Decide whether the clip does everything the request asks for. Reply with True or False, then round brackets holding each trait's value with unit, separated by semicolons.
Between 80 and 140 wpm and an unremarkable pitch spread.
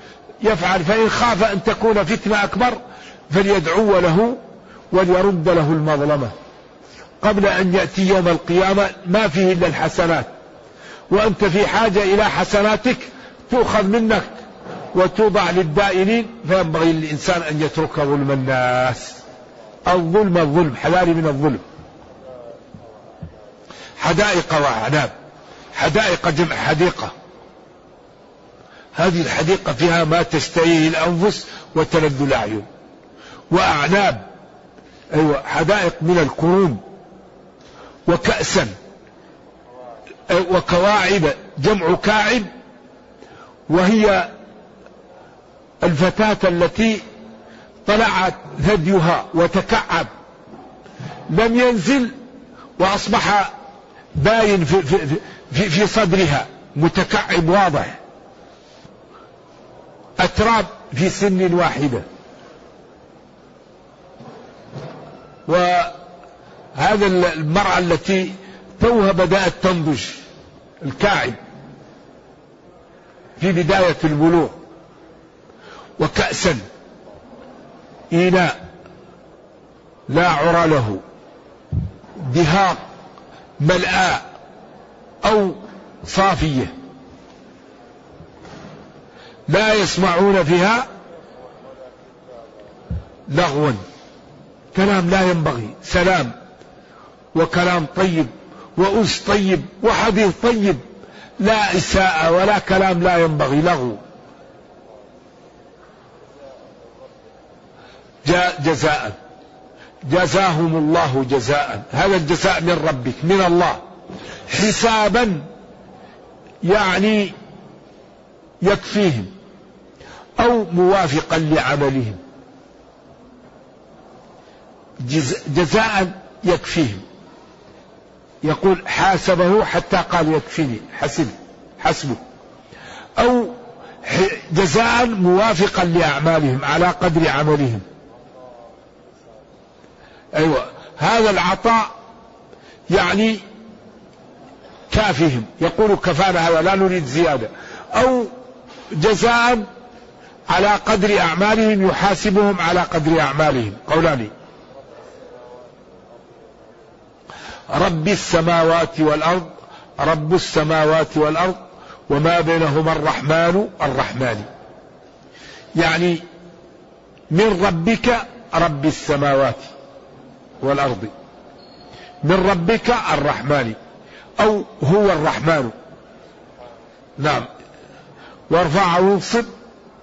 False (70 wpm; 4.4 semitones)